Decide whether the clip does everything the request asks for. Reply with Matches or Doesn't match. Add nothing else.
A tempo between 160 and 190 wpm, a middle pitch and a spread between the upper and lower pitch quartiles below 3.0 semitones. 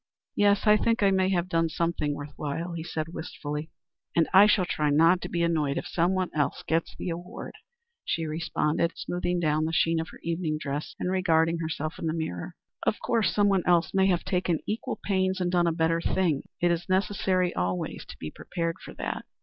Doesn't match